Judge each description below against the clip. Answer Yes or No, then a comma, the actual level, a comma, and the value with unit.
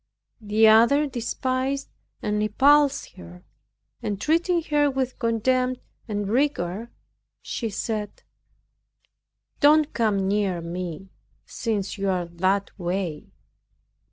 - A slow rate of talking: Yes, slow, 100 wpm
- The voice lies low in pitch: No, high, 220 Hz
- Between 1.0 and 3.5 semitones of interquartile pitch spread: No, wide, 5.4 semitones